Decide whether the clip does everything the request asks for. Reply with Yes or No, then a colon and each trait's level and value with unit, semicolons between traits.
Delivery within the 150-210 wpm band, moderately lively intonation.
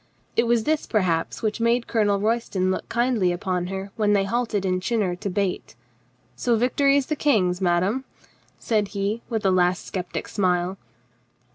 Yes: average, 165 wpm; average, 4.1 semitones